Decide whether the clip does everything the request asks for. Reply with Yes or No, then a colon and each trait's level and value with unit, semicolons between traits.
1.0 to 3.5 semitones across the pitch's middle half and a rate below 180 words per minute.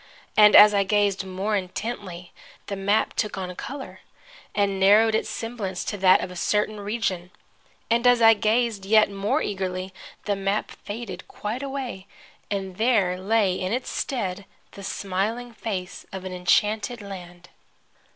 Yes: average, 2.7 semitones; average, 150 wpm